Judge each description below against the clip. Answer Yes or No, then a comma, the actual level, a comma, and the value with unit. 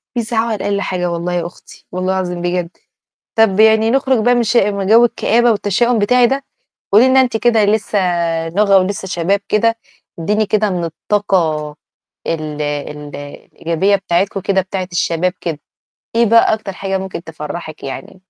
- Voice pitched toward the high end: Yes, high, 195 Hz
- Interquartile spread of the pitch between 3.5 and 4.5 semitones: Yes, average, 4.1 semitones